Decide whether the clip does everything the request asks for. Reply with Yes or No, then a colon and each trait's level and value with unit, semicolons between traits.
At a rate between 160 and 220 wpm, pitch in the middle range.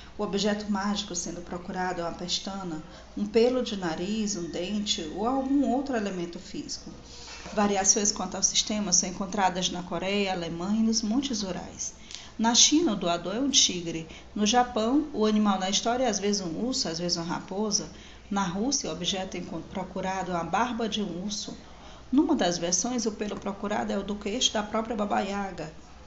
No: fast, 185 wpm; high, 200 Hz